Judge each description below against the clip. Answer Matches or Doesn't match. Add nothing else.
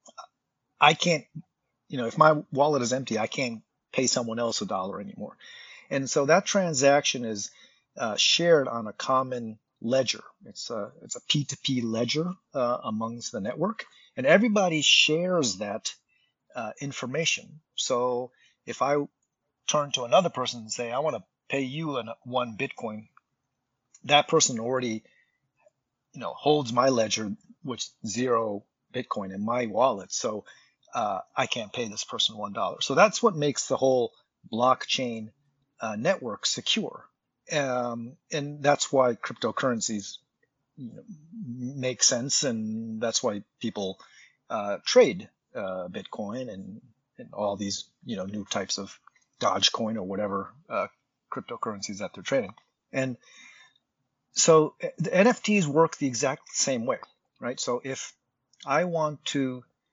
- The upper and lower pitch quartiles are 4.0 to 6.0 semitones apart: Matches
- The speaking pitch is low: Matches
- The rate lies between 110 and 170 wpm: Matches